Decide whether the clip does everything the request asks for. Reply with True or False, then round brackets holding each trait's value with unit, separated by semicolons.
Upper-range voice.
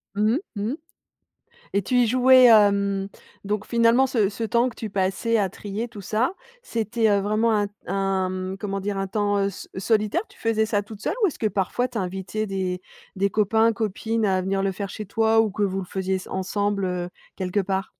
True (205 Hz)